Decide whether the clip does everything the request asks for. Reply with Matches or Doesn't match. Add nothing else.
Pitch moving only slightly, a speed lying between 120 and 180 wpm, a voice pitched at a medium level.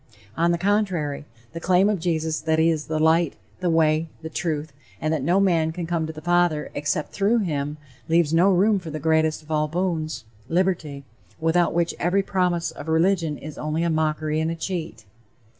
Doesn't match